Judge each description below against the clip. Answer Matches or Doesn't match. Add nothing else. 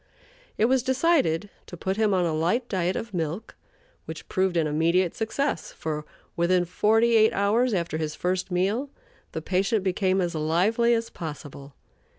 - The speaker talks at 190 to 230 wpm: Doesn't match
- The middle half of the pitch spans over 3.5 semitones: Matches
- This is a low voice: Doesn't match